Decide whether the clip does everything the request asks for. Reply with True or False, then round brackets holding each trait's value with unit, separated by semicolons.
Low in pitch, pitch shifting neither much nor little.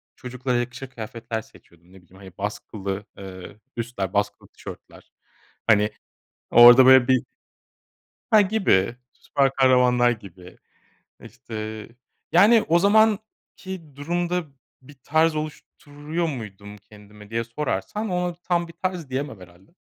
False (125 Hz; 7.7 semitones)